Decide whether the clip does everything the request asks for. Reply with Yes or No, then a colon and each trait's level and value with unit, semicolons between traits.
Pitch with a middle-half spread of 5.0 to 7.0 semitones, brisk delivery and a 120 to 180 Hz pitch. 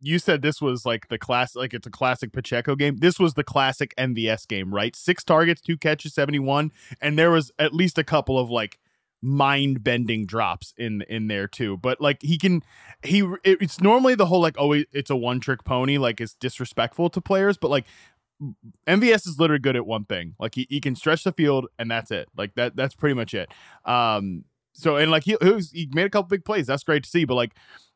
Yes: wide, 5.4 semitones; fast, 230 wpm; medium, 140 Hz